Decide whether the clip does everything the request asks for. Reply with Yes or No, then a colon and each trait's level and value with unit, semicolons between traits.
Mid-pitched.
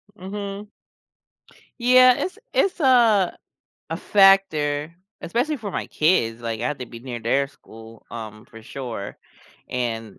Yes: medium, 145 Hz